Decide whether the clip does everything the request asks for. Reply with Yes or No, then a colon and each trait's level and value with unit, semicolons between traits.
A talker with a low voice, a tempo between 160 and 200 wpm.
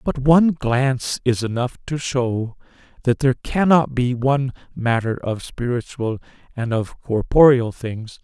No: low, 125 Hz; average, 140 wpm